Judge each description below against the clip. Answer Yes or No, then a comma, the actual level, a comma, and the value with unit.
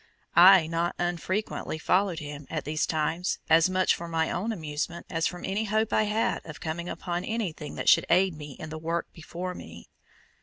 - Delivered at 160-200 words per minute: Yes, average, 190 wpm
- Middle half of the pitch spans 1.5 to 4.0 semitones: Yes, average, 2.8 semitones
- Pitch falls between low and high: Yes, medium, 170 Hz